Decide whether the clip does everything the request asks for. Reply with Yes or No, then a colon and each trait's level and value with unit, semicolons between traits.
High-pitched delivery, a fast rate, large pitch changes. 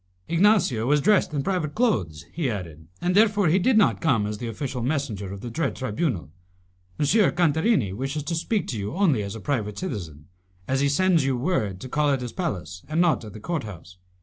No: low, 135 Hz; fast, 210 wpm; wide, 8.6 semitones